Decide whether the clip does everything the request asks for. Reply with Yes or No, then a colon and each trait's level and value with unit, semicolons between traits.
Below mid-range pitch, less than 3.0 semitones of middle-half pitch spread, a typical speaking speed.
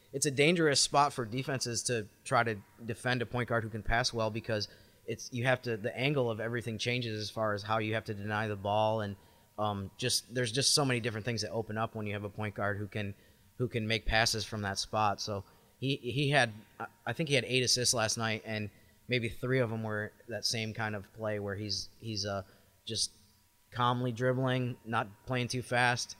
No: low, 110 Hz; narrow, 2.6 semitones; fast, 225 wpm